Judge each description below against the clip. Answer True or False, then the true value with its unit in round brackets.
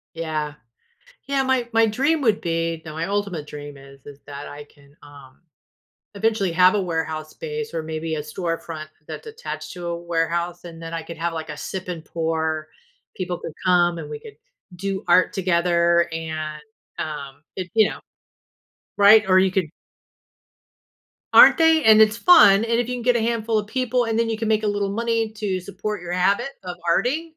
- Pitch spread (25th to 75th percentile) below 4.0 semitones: False (5.4 semitones)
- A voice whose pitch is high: False (180 Hz)